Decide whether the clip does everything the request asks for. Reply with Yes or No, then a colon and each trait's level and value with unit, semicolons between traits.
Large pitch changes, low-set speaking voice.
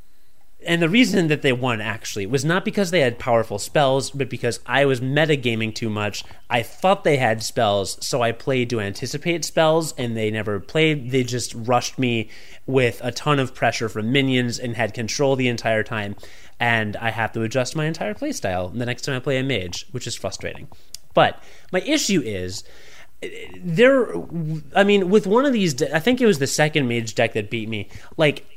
Yes: wide, 5.8 semitones; low, 125 Hz